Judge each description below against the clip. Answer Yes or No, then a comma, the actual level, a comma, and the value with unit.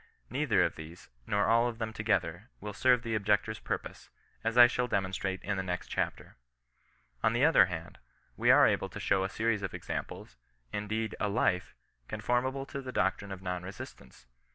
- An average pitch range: Yes, average, 3.5 semitones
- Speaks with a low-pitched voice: Yes, low, 105 Hz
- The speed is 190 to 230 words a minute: Yes, average, 195 wpm